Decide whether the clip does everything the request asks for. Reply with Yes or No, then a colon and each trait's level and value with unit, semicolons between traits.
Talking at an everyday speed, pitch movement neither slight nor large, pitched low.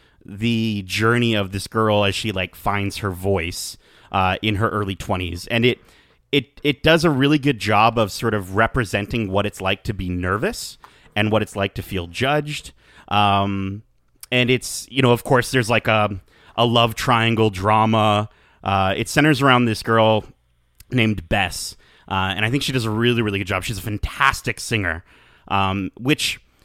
Yes: average, 180 wpm; average, 3.3 semitones; low, 110 Hz